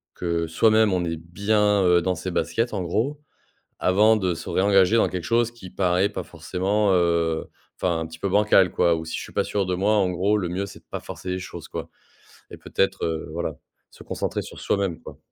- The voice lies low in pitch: Yes, very low, 95 Hz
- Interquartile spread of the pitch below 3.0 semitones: No, average, 3.3 semitones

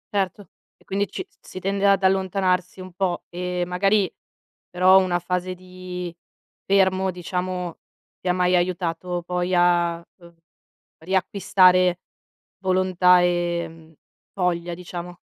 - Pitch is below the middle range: No, medium, 180 Hz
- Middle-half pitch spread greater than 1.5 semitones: No, narrow, 1.1 semitones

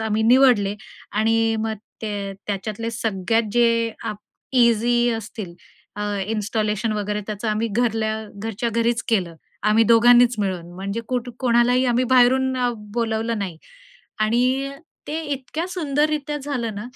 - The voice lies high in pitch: Yes, high, 230 Hz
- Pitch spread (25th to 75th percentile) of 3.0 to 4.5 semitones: No, narrow, 2.5 semitones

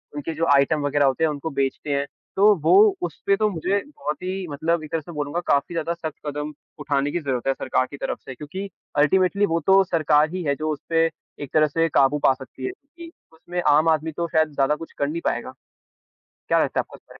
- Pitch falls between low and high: Yes, medium, 155 Hz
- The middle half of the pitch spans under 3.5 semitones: Yes, average, 2.9 semitones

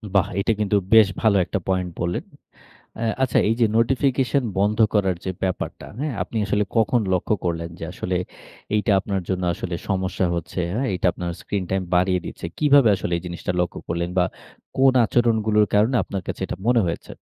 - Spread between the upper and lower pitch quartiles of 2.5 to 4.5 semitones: Yes, average, 4.0 semitones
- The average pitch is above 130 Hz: No, low, 100 Hz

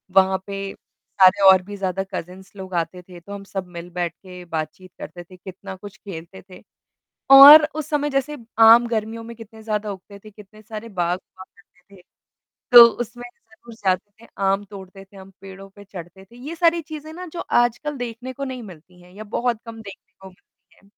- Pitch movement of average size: Yes, average, 3.8 semitones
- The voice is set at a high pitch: Yes, high, 200 Hz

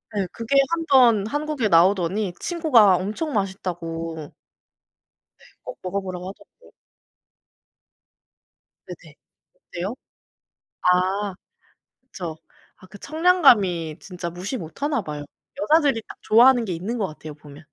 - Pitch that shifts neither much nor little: No, wide, 6.5 semitones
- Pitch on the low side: No, high, 200 Hz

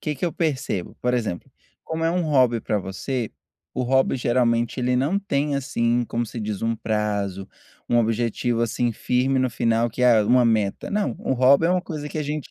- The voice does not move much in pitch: No, average, 3.4 semitones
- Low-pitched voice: Yes, low, 125 Hz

